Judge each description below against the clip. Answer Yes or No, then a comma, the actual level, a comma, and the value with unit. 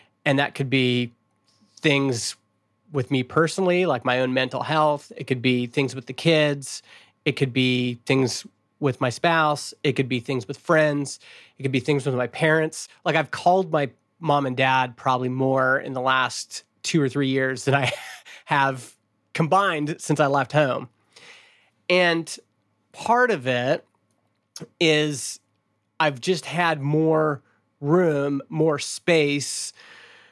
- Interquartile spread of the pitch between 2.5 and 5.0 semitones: Yes, average, 3.5 semitones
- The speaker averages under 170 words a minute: Yes, average, 150 wpm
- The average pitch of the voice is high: No, medium, 140 Hz